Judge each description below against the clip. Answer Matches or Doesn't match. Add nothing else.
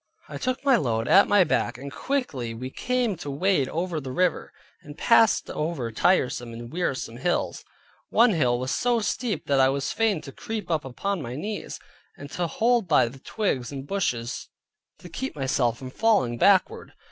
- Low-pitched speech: Doesn't match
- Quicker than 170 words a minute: Matches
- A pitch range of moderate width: Doesn't match